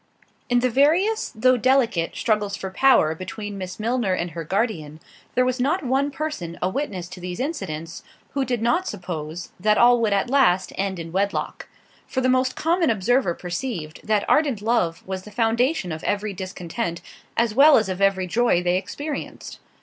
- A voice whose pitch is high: Yes, high, 210 Hz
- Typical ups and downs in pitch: No, wide, 5.9 semitones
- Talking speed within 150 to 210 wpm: Yes, average, 175 wpm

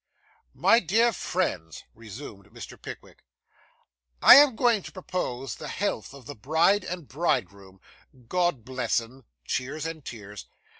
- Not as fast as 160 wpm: Yes, slow, 135 wpm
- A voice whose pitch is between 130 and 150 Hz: Yes, medium, 140 Hz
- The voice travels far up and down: Yes, wide, 8.2 semitones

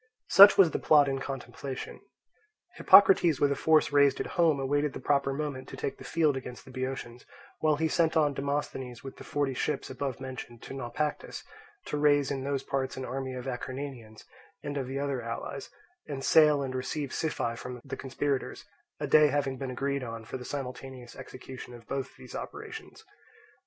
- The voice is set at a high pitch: No, low, 135 Hz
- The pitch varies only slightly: Yes, narrow, 2.1 semitones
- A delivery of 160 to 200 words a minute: Yes, average, 185 wpm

